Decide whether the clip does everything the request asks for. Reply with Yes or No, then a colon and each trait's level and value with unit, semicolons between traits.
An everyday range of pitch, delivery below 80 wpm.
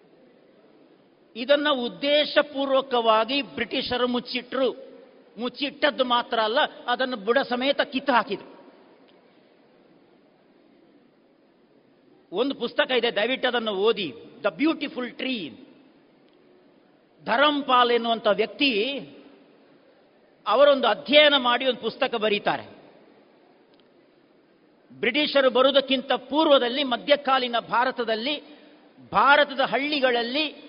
Yes: average, 3.0 semitones; average, 70 wpm